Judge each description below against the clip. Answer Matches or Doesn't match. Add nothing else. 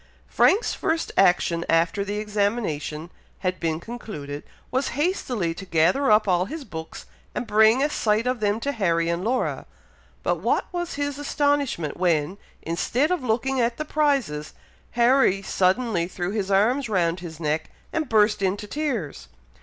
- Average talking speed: Matches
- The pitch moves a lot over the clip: Matches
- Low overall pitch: Doesn't match